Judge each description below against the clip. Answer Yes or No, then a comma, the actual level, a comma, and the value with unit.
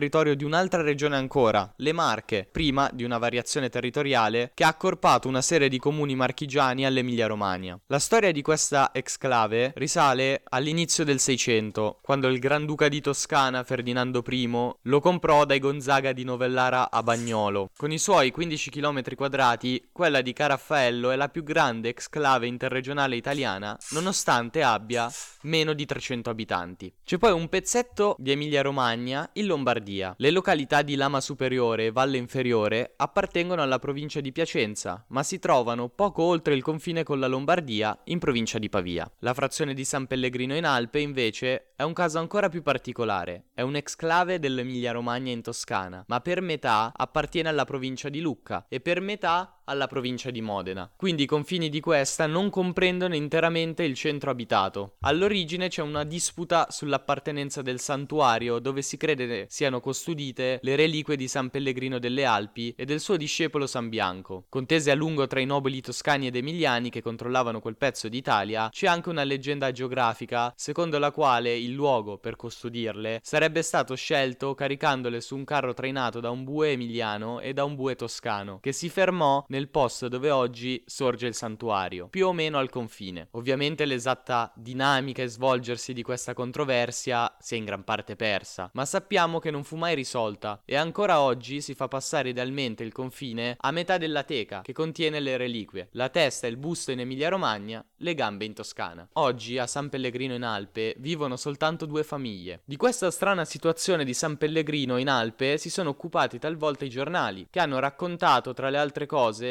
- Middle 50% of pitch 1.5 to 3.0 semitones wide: No, average, 4.0 semitones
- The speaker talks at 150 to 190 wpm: Yes, fast, 170 wpm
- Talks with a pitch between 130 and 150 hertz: Yes, low, 135 Hz